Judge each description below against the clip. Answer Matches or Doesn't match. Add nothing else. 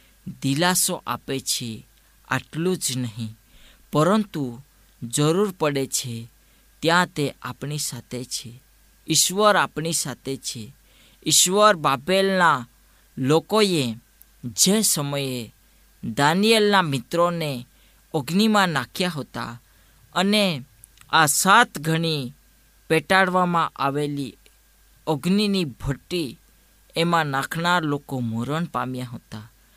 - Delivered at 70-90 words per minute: Matches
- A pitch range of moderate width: Doesn't match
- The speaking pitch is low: Doesn't match